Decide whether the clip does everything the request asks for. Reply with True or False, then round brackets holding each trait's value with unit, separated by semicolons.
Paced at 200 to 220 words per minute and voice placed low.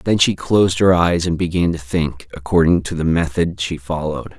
True (205 wpm; 85 Hz)